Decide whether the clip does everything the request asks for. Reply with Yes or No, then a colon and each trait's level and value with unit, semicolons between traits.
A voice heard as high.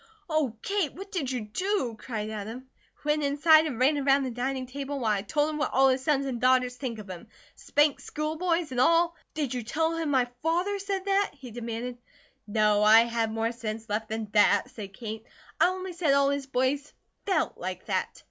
Yes: very high, 265 Hz